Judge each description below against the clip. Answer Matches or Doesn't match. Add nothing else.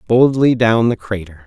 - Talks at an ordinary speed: Matches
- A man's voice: Matches